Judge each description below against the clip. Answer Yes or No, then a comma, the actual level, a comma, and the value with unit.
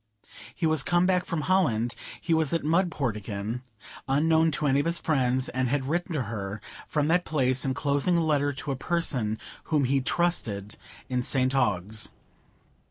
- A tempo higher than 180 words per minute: No, average, 170 wpm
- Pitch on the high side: No, medium, 140 Hz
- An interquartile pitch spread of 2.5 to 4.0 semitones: No, average, 4.6 semitones